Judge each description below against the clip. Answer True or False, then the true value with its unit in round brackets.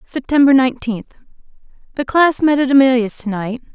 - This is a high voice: True (255 Hz)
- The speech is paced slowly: True (130 wpm)